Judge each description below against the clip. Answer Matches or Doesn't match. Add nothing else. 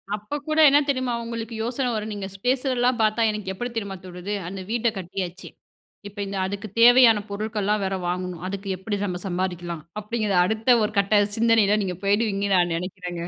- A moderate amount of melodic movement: Matches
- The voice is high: Matches